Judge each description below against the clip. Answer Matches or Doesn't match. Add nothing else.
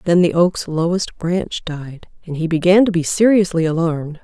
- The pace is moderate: Matches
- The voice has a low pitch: Doesn't match